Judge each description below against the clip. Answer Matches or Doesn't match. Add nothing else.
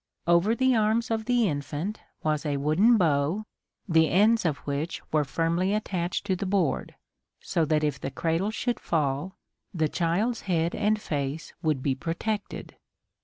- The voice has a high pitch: Doesn't match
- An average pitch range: Doesn't match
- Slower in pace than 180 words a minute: Matches